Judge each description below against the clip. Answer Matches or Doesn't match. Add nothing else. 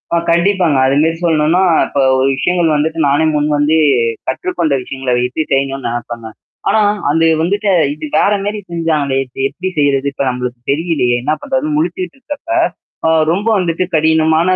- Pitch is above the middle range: Doesn't match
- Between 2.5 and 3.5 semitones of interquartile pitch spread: Doesn't match